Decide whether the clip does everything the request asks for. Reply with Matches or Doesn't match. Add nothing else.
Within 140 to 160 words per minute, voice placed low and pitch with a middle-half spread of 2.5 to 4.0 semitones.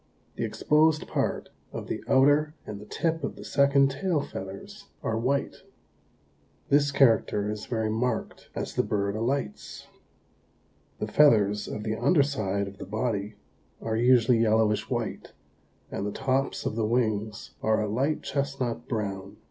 Doesn't match